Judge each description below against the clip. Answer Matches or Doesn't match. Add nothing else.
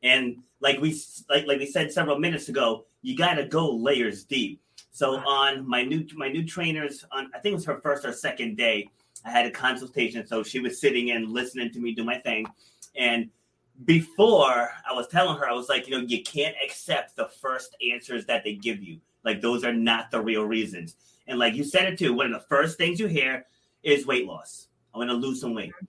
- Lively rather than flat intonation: Doesn't match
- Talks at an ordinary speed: Doesn't match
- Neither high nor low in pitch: Doesn't match